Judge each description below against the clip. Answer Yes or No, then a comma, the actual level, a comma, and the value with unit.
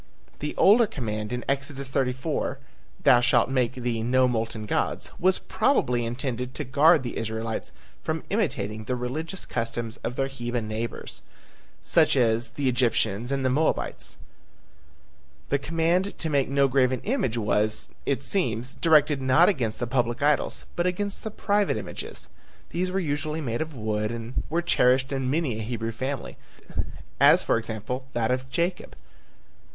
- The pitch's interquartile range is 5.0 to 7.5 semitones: No, average, 4.6 semitones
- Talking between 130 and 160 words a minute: Yes, average, 155 wpm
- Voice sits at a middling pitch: No, low, 130 Hz